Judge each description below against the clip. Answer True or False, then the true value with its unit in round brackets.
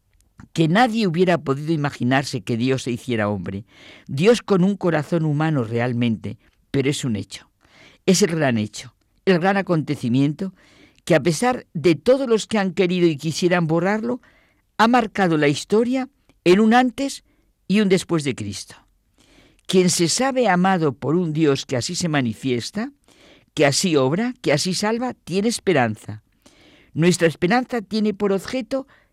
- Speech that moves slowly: False (155 wpm)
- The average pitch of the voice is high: False (170 Hz)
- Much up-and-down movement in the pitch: True (7.4 semitones)